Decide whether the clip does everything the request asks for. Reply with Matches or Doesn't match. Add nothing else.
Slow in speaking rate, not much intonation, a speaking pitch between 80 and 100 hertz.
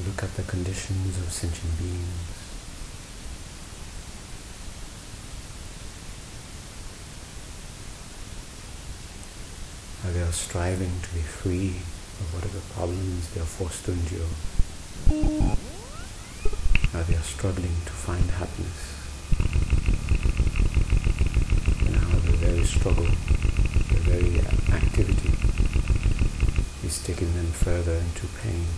Matches